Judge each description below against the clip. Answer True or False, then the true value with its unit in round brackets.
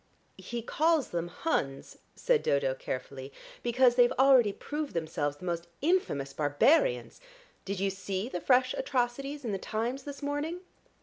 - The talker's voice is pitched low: False (240 Hz)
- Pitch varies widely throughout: True (8.8 semitones)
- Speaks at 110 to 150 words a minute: True (145 wpm)